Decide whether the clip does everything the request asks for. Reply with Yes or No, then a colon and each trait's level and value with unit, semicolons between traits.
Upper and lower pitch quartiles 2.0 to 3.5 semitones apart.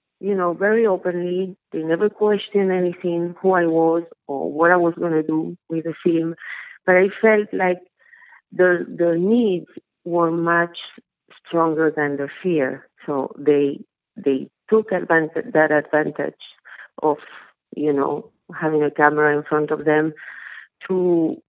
Yes: average, 2.8 semitones